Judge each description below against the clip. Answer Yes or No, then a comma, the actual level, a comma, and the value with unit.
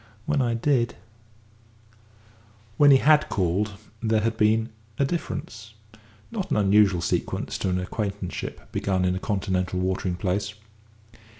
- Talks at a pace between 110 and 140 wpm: Yes, slow, 135 wpm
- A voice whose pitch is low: Yes, low, 105 Hz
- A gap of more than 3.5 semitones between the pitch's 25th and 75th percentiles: No, average, 3.2 semitones